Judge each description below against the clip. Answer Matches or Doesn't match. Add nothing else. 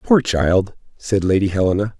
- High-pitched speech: Doesn't match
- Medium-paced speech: Matches